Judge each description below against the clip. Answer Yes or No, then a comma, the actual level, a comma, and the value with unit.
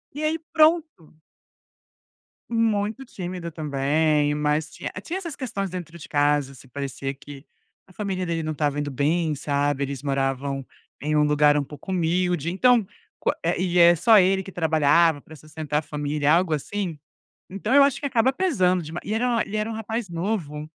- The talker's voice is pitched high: No, medium, 165 Hz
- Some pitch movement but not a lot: No, wide, 5.8 semitones